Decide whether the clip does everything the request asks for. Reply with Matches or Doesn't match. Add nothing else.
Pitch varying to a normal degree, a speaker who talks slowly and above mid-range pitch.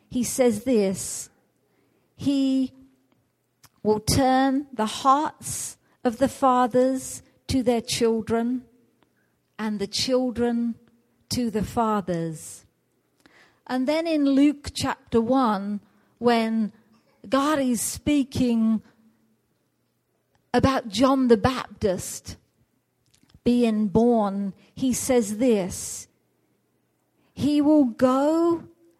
Matches